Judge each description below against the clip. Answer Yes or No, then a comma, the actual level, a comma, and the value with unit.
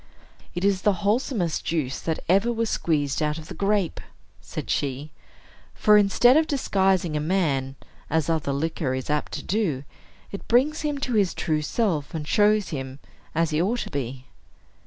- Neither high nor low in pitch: Yes, medium, 170 Hz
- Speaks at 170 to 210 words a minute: Yes, average, 175 wpm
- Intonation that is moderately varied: No, wide, 5.8 semitones